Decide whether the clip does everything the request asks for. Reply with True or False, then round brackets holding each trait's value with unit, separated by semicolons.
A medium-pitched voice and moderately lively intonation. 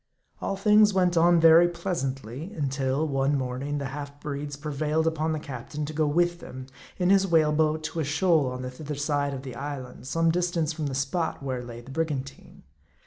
True (150 Hz; 3.3 semitones)